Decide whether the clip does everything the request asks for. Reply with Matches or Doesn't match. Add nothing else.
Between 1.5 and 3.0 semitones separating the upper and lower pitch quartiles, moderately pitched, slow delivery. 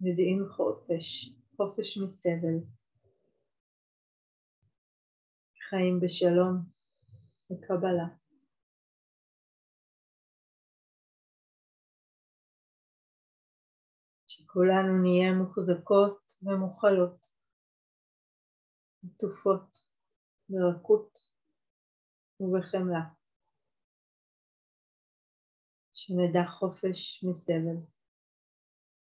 Matches